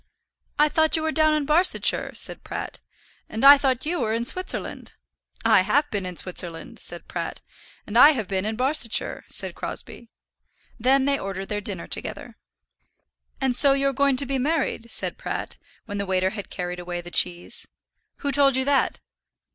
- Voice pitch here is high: Yes, very high, 255 Hz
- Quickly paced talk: No, average, 180 wpm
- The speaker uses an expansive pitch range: Yes, wide, 6.3 semitones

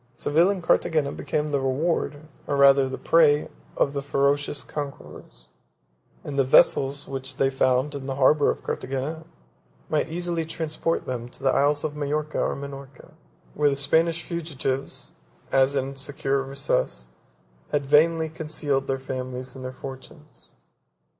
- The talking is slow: No, average, 155 wpm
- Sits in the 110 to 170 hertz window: Yes, medium, 140 Hz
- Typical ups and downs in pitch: No, narrow, 2.3 semitones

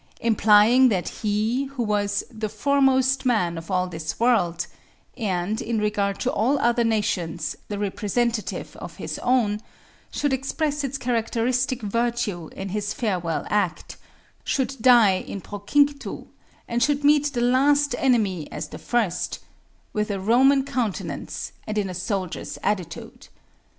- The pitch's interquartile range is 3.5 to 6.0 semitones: Yes, average, 4.4 semitones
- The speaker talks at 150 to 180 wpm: No, average, 140 wpm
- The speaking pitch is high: Yes, high, 220 Hz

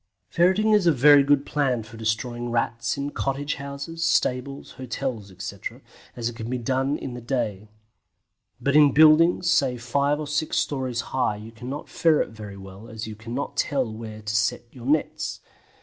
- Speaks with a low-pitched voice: Yes, low, 130 Hz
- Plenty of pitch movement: No, average, 4.2 semitones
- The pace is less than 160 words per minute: No, average, 175 wpm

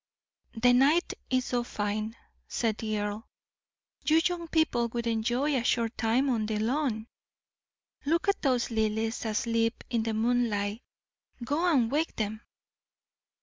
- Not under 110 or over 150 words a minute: Yes, average, 140 wpm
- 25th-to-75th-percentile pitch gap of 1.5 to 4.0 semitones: Yes, average, 3.2 semitones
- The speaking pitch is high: Yes, high, 235 Hz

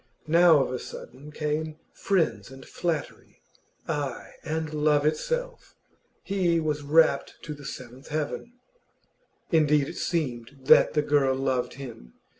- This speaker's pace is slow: Yes, slow, 130 wpm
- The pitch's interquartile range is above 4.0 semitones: No, average, 2.9 semitones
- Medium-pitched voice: Yes, medium, 150 Hz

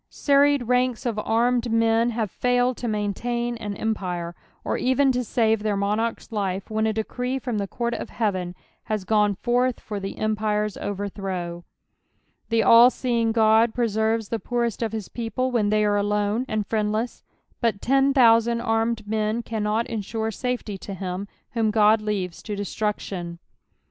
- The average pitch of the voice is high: Yes, high, 220 Hz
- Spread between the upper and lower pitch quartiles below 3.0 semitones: Yes, narrow, 2.4 semitones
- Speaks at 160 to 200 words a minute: Yes, average, 165 wpm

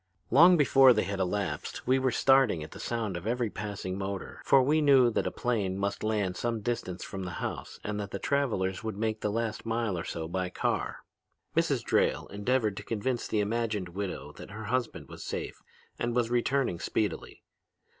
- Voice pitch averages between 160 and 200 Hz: No, low, 110 Hz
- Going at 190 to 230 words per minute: Yes, average, 195 wpm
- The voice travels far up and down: No, average, 3.9 semitones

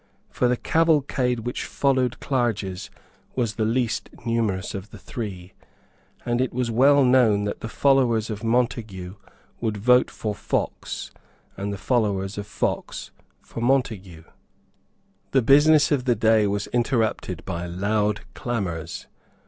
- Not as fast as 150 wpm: Yes, slow, 135 wpm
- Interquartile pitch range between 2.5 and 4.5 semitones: Yes, average, 3.7 semitones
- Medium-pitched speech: No, low, 115 Hz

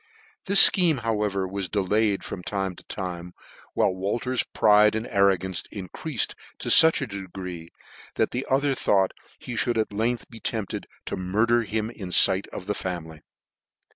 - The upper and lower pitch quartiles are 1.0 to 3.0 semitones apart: No, average, 3.7 semitones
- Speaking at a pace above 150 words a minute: Yes, average, 165 wpm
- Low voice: Yes, low, 105 Hz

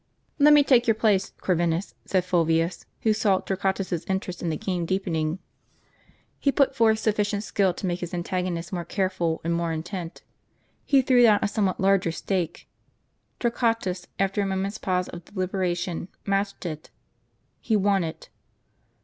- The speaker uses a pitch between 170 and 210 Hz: Yes, high, 190 Hz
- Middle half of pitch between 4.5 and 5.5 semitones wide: No, average, 2.9 semitones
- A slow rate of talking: No, average, 160 wpm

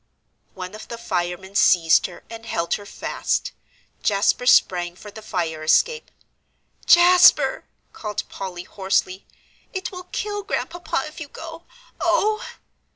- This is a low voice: No, high, 210 Hz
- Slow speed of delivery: Yes, slow, 130 wpm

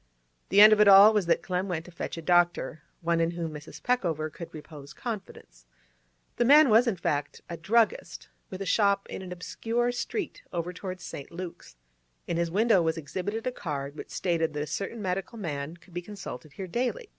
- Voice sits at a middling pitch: Yes, medium, 180 Hz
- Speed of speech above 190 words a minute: Yes, fast, 205 wpm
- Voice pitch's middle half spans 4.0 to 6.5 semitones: Yes, average, 4.4 semitones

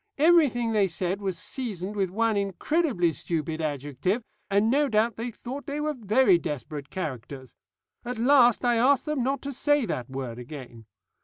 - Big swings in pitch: Yes, wide, 8.2 semitones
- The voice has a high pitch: Yes, high, 210 Hz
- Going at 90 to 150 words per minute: No, average, 165 wpm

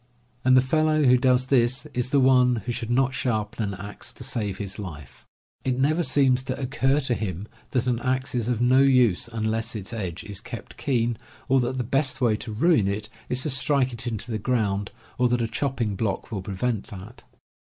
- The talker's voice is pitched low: Yes, low, 120 Hz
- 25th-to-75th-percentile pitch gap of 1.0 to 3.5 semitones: Yes, average, 3.2 semitones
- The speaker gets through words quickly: Yes, fast, 210 wpm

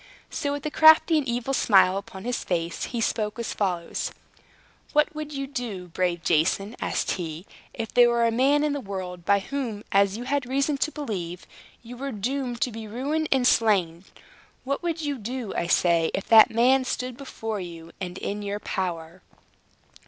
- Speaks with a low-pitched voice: No, high, 225 Hz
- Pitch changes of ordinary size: No, wide, 6.2 semitones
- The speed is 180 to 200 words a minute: Yes, average, 185 wpm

